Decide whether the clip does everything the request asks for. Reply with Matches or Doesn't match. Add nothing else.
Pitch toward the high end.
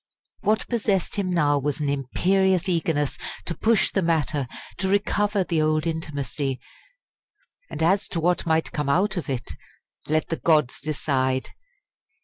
Doesn't match